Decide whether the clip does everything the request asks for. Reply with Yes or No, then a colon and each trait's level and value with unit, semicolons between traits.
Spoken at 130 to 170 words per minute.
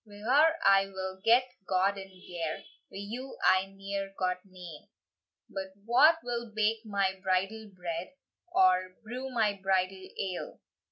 Yes: average, 145 wpm